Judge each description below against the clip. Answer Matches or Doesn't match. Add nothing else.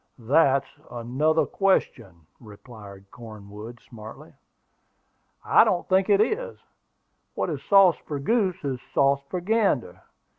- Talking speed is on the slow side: Matches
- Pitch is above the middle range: Doesn't match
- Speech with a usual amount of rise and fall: Doesn't match